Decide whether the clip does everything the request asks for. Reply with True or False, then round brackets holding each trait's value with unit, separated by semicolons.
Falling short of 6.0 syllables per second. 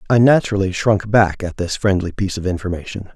False (6.2 syllables/s)